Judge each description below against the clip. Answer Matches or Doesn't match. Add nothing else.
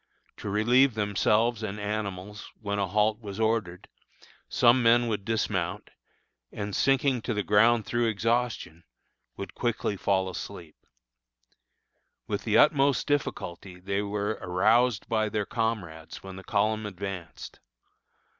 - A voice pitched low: Matches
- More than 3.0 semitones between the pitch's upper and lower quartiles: Doesn't match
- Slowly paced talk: Matches